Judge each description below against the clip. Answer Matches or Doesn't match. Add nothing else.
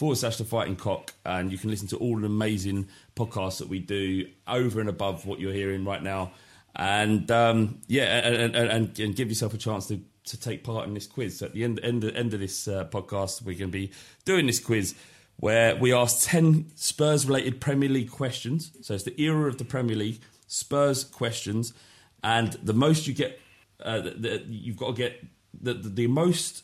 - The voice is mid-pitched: Doesn't match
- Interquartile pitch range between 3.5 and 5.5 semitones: Matches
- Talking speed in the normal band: Doesn't match